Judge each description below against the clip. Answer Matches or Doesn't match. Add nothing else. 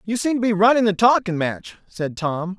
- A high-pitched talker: Matches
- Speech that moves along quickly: Matches